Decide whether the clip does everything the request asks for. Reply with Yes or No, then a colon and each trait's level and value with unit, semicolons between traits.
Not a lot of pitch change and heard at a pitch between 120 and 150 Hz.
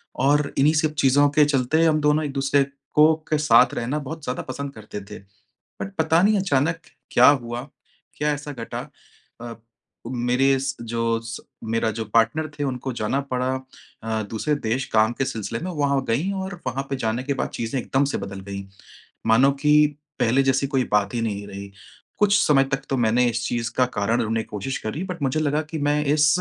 No: average, 4.3 semitones; low, 135 Hz